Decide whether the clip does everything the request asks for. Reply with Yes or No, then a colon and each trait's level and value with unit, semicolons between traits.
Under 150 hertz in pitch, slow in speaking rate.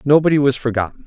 No: low, 135 Hz; average, 170 wpm